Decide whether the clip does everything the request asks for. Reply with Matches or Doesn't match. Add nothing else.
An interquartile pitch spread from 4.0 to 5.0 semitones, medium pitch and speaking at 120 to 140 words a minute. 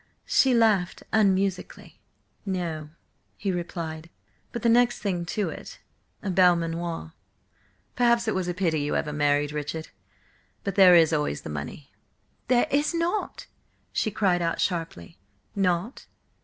Matches